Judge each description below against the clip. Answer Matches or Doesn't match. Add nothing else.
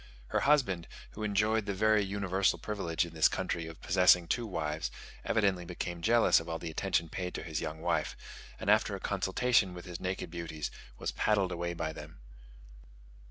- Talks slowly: Doesn't match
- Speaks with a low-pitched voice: Matches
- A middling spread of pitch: Matches